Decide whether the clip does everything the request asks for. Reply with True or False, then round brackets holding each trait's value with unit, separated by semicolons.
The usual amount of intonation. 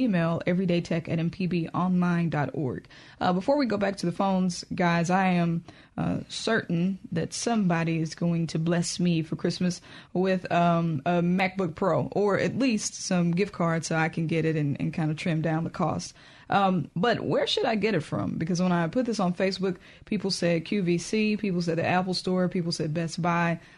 False (2.3 semitones)